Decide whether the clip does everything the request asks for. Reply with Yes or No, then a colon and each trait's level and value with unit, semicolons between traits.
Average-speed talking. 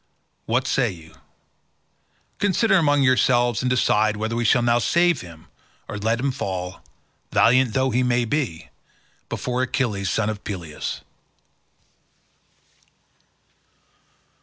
No: slow, 110 wpm